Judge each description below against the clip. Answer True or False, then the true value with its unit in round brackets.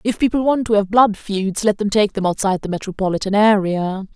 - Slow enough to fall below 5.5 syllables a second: False (5.7 syllables/s)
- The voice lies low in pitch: False (205 Hz)